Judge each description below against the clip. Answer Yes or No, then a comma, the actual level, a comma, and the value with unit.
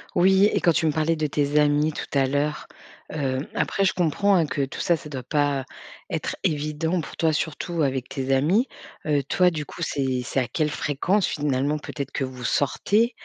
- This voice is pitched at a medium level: Yes, medium, 150 Hz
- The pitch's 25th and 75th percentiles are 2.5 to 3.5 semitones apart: Yes, average, 3.2 semitones